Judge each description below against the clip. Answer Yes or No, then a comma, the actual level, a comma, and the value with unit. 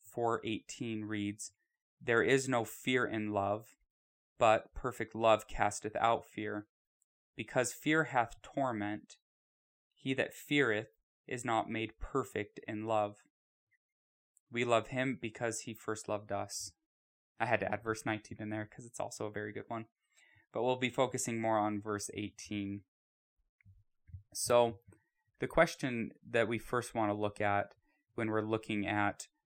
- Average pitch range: No, narrow, 2.3 semitones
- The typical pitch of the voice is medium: No, low, 110 Hz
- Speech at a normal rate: Yes, average, 150 wpm